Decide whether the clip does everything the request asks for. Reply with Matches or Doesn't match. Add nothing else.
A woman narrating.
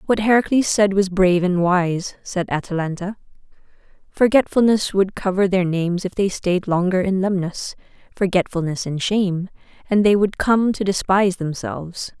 Matches